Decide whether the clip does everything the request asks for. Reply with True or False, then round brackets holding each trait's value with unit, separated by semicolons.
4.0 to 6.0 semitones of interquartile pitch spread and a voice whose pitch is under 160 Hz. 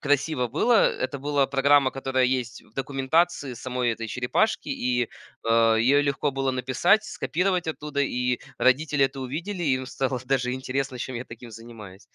False (2.5 semitones; 135 Hz)